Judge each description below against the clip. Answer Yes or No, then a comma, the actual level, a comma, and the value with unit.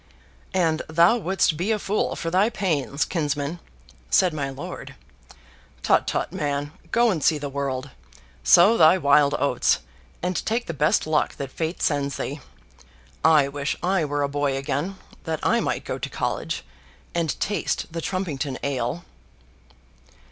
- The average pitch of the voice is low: No, medium, 155 Hz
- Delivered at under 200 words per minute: Yes, average, 155 wpm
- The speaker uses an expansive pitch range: No, average, 4.2 semitones